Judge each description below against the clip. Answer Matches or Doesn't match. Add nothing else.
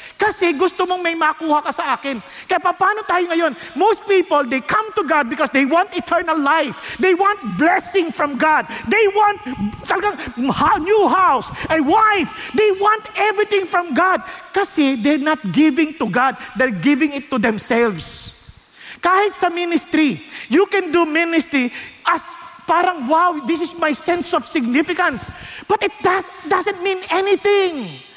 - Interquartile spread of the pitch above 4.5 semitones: Doesn't match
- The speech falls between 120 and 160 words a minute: Matches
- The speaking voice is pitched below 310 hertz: Doesn't match